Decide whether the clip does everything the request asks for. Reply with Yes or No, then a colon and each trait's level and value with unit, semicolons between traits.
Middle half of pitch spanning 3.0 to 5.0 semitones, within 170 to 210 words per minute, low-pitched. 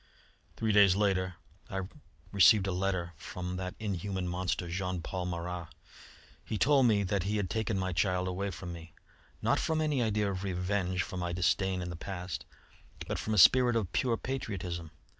No: narrow, 2.4 semitones; average, 180 wpm; very low, 95 Hz